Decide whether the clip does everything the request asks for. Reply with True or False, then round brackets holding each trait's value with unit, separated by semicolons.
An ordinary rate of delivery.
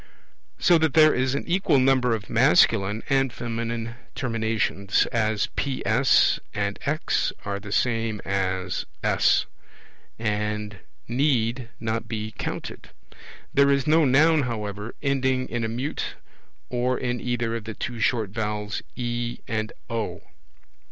False (130 wpm)